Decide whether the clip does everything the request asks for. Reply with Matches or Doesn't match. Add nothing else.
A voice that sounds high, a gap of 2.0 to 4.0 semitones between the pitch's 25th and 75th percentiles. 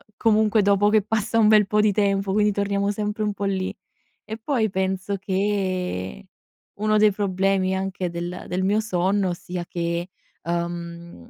Matches